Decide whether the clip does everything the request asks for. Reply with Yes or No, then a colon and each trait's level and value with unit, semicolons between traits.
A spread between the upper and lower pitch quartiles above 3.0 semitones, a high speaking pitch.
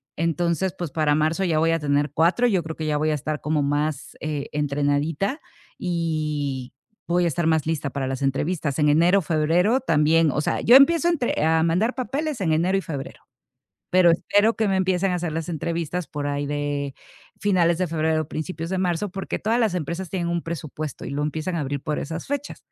No: average, 3.4 semitones; medium, 165 Hz